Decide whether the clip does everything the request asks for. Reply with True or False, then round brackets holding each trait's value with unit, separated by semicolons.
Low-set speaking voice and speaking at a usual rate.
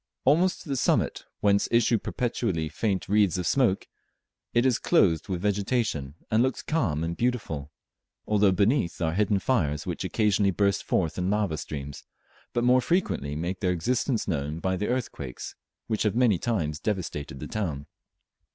True (100 Hz; 160 wpm)